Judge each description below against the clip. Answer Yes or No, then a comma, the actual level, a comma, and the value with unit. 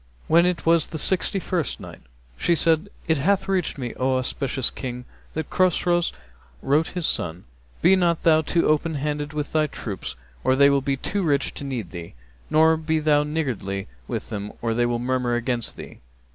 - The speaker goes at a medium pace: Yes, average, 185 wpm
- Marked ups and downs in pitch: No, average, 4.5 semitones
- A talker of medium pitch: Yes, medium, 150 Hz